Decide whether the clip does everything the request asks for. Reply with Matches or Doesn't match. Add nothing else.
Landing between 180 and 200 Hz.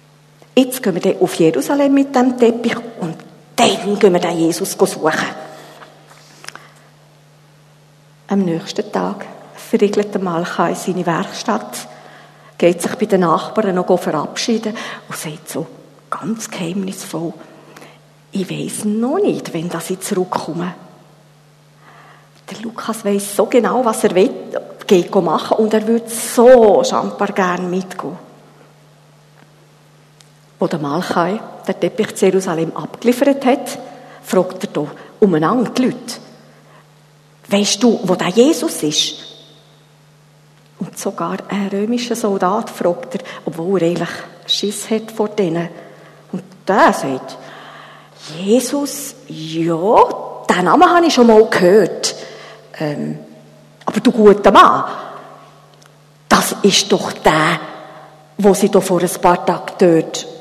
Matches